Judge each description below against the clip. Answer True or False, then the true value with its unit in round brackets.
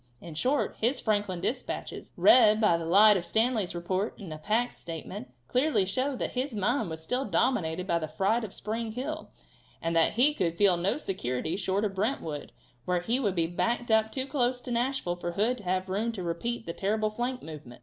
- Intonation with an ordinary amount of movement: False (5.7 semitones)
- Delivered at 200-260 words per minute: True (205 wpm)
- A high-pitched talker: True (205 Hz)